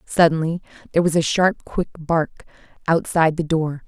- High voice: No, medium, 160 Hz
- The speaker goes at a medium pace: Yes, average, 155 wpm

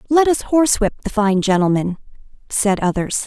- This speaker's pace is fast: No, average, 145 wpm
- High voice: Yes, high, 220 Hz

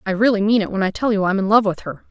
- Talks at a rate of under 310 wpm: No, fast, 370 wpm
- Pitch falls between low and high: No, high, 205 Hz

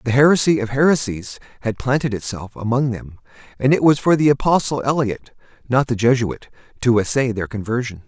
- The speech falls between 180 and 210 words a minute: No, average, 170 wpm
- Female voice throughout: No, male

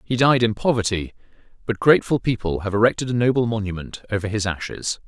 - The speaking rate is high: No, average, 180 wpm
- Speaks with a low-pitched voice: Yes, low, 110 Hz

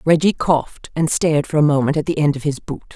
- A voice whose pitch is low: No, medium, 150 Hz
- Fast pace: Yes, fast, 265 wpm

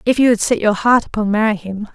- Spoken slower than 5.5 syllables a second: No, 6.0 syllables/s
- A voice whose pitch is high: Yes, high, 215 Hz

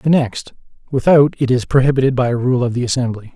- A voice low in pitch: Yes, low, 130 Hz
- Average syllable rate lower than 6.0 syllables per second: No, 6.2 syllables/s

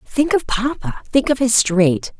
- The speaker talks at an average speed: Yes, average, 190 wpm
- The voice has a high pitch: Yes, high, 235 Hz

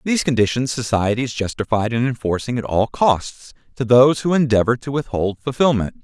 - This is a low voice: Yes, low, 120 Hz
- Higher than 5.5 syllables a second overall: Yes, 5.7 syllables/s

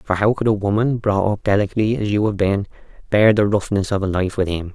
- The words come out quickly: Yes, fast, 255 wpm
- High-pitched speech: No, low, 100 Hz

